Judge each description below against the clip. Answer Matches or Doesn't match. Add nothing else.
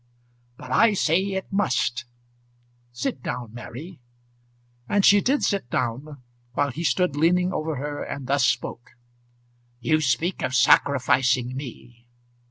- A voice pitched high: Doesn't match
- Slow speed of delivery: Matches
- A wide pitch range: Matches